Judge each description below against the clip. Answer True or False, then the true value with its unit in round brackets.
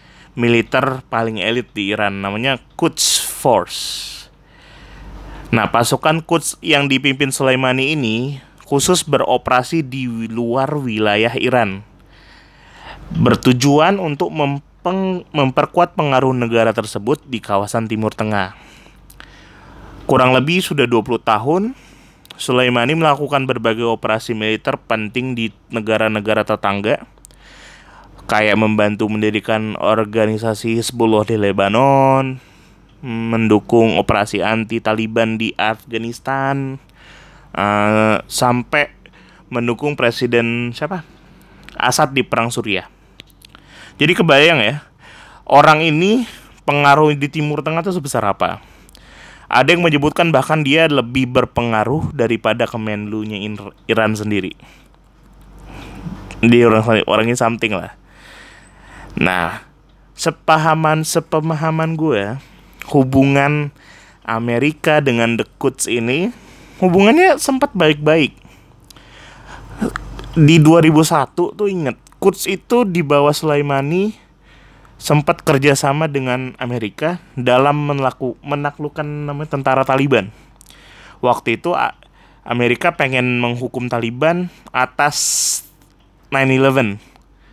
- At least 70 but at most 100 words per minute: True (95 wpm)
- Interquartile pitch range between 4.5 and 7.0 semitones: True (4.8 semitones)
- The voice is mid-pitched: False (130 Hz)